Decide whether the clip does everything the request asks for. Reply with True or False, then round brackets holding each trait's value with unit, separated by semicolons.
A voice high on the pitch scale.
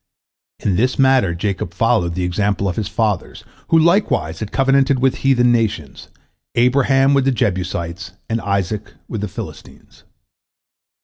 False (110 Hz)